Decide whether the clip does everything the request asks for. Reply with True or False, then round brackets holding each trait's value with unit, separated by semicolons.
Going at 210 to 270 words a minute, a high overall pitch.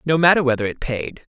False (220 wpm; 135 Hz)